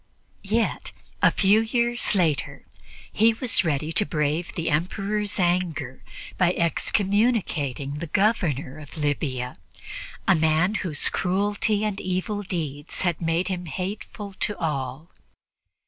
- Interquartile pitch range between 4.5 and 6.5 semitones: Yes, average, 5.1 semitones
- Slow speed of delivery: Yes, slow, 120 wpm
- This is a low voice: No, medium, 175 Hz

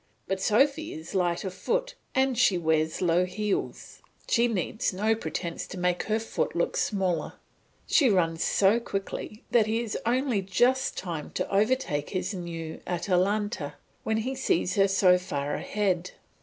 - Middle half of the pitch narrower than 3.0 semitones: No, average, 3.9 semitones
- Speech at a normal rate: Yes, average, 155 wpm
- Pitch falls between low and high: No, high, 195 Hz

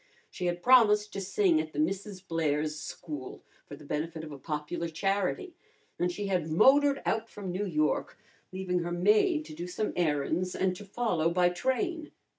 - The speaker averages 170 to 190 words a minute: Yes, average, 180 wpm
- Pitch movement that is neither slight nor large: Yes, average, 4.6 semitones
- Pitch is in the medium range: Yes, medium, 180 Hz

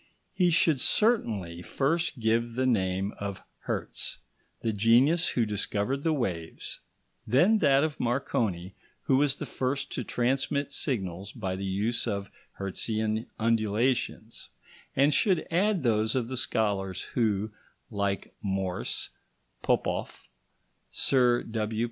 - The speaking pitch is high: No, low, 115 Hz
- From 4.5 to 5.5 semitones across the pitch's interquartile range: Yes, average, 5.1 semitones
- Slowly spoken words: Yes, slow, 125 wpm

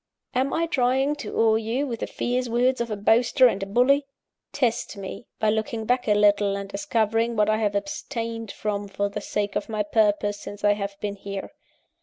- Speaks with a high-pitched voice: Yes, high, 220 Hz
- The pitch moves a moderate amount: Yes, average, 3.1 semitones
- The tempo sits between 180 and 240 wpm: Yes, fast, 205 wpm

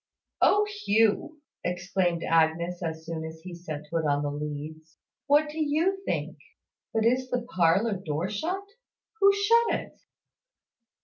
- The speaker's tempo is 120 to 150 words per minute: Yes, average, 140 wpm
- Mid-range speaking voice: Yes, medium, 180 Hz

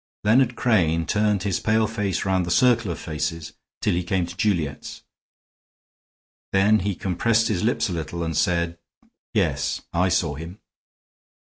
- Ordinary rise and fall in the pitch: Yes, average, 4.0 semitones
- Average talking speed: Yes, average, 150 wpm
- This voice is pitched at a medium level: No, very low, 95 Hz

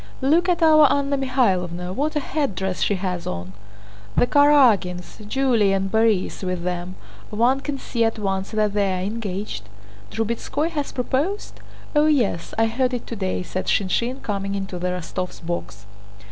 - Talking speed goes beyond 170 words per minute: No, average, 145 wpm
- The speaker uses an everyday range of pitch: No, wide, 6.5 semitones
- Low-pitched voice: No, high, 215 Hz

